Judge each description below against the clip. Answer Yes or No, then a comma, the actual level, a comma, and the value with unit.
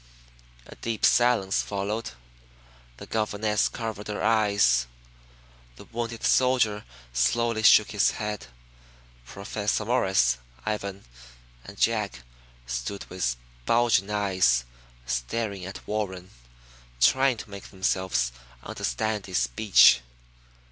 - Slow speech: Yes, slow, 100 wpm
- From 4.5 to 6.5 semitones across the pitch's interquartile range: No, average, 3.0 semitones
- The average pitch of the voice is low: Yes, low, 100 Hz